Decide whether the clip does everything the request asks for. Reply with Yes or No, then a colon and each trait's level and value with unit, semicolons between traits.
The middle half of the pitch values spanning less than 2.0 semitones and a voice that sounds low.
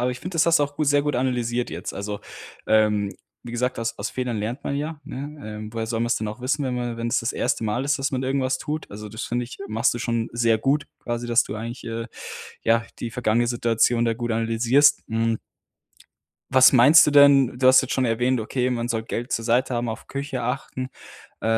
No: narrow, 2.5 semitones; low, 120 Hz